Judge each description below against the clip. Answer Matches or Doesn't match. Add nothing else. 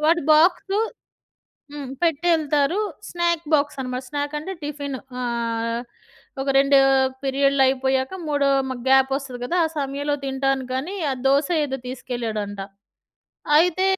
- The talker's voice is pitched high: Matches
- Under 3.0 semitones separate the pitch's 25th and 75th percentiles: Matches